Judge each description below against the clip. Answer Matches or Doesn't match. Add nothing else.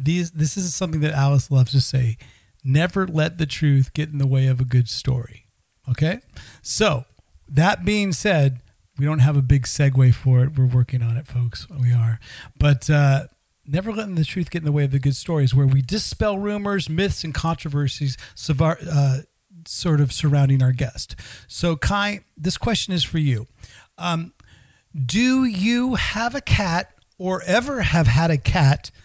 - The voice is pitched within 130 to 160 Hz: Matches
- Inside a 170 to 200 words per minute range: Matches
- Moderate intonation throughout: Matches